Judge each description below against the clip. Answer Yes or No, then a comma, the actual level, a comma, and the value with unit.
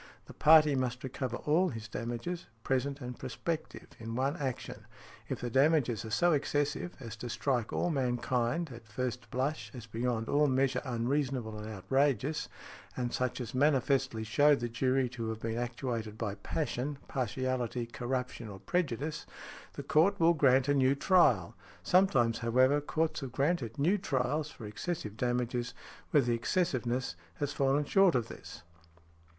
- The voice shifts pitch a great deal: No, average, 3.7 semitones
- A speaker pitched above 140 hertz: No, low, 130 Hz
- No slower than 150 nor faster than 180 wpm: Yes, average, 155 wpm